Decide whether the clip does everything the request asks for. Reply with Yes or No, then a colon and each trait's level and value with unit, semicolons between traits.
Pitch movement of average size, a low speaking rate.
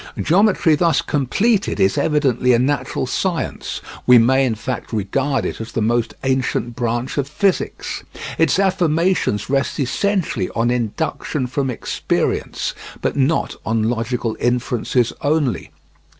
Yes: average, 4.8 semitones; slow, 130 wpm